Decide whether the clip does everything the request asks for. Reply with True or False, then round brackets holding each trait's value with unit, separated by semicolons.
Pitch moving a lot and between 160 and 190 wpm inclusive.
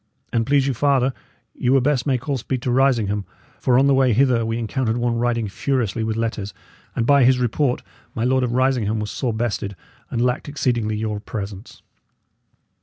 False (2.9 semitones; 185 wpm)